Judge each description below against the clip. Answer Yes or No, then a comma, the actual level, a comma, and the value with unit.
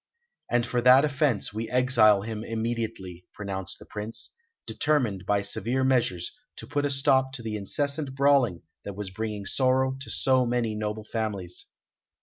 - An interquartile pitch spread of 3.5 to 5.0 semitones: Yes, average, 4.1 semitones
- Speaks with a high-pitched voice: No, low, 115 Hz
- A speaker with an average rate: Yes, average, 155 wpm